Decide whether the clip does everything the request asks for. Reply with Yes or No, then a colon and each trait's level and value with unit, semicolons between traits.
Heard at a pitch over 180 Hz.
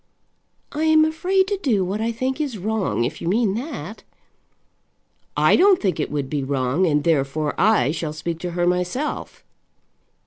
Yes: high, 190 Hz